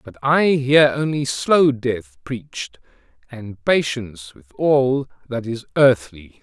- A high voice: No, low, 125 Hz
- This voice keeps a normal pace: No, slow, 130 wpm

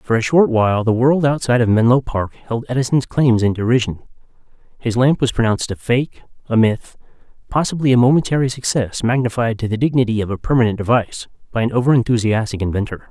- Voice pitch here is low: Yes, low, 120 Hz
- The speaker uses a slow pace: No, average, 180 wpm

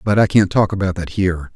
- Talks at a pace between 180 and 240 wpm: No, fast, 270 wpm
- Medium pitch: No, very low, 95 Hz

